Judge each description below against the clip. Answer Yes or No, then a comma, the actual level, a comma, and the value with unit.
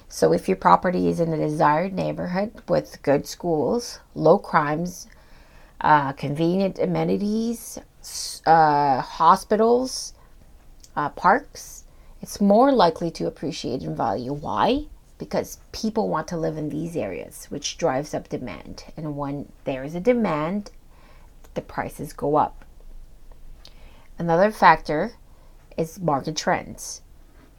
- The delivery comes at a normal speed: No, slow, 120 wpm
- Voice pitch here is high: No, medium, 160 Hz